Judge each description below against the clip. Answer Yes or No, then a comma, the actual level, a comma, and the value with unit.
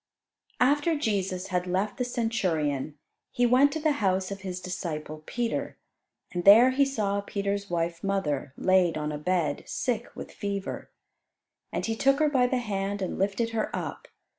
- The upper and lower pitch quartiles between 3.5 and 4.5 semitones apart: No, average, 5.1 semitones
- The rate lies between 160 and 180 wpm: Yes, average, 165 wpm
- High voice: Yes, high, 200 Hz